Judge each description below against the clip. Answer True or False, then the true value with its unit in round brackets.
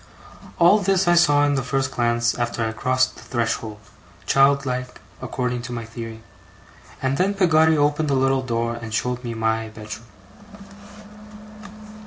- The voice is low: True (125 Hz)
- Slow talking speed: False (155 wpm)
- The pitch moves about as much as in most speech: True (3.7 semitones)